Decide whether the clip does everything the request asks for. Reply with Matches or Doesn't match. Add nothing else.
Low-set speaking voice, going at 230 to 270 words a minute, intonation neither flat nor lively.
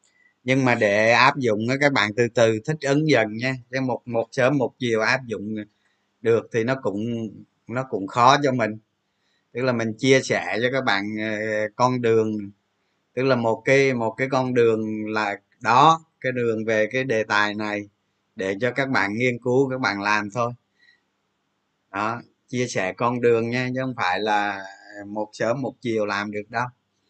Doesn't match